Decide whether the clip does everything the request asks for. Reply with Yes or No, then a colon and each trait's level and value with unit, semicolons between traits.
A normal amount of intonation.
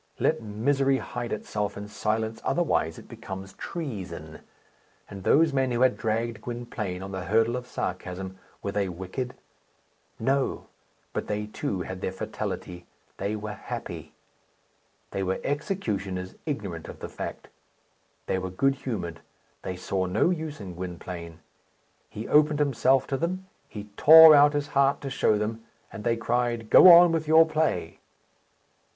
No: wide, 6.4 semitones